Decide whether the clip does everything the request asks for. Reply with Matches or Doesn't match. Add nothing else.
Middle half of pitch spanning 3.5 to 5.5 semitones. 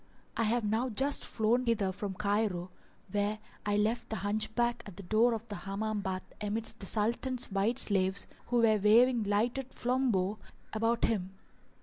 Doesn't match